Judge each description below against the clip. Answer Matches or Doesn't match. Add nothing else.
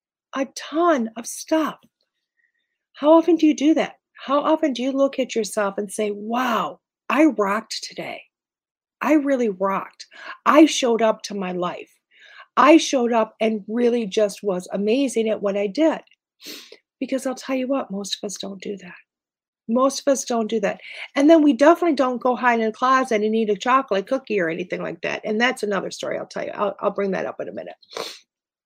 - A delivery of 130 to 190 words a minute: Doesn't match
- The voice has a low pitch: Doesn't match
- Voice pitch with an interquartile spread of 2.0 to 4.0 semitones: Doesn't match